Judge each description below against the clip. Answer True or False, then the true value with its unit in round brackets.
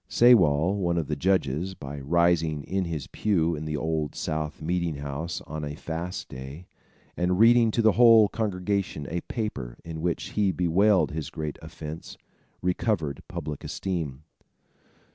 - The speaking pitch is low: True (85 Hz)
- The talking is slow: False (150 wpm)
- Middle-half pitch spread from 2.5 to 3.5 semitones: False (3.9 semitones)